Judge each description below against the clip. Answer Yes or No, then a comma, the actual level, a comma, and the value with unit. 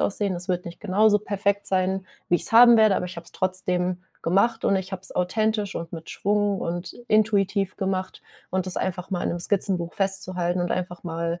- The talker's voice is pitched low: No, medium, 185 Hz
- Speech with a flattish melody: Yes, narrow, 2.2 semitones